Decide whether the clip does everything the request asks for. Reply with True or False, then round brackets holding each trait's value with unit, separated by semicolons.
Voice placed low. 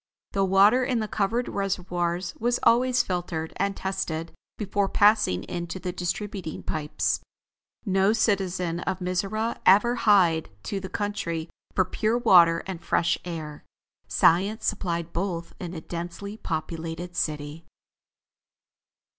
False (185 Hz)